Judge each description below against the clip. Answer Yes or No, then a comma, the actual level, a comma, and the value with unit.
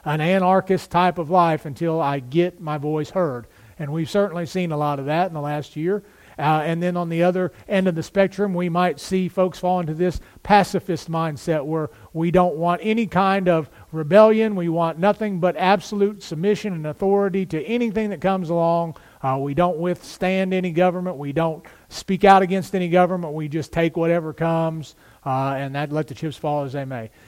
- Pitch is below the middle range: No, medium, 175 Hz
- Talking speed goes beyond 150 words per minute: Yes, average, 200 wpm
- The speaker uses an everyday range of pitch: Yes, average, 3.4 semitones